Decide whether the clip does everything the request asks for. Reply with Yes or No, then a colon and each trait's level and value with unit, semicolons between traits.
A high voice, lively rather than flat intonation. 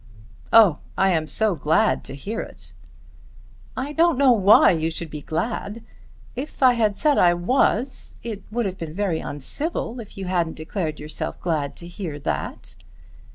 Yes: high, 195 Hz; wide, 6.4 semitones